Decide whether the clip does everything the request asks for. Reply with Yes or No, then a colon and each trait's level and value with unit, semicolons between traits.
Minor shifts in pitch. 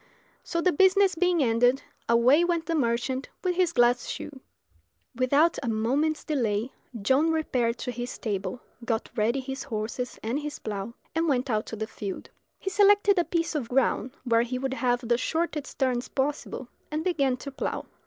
No: average, 5.2 semitones